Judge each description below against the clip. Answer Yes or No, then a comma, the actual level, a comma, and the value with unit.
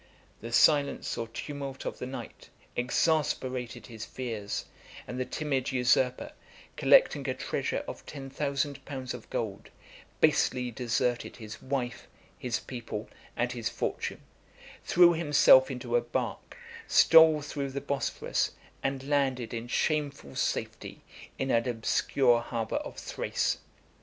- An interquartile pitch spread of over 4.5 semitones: No, average, 3.1 semitones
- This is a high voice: No, low, 130 Hz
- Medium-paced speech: No, slow, 130 wpm